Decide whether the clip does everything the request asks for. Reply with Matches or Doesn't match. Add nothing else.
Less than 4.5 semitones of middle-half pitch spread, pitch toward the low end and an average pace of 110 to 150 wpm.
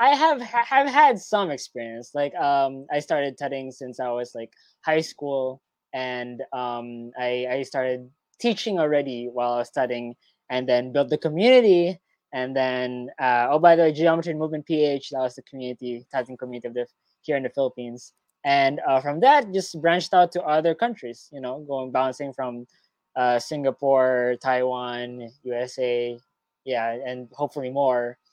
Doesn't match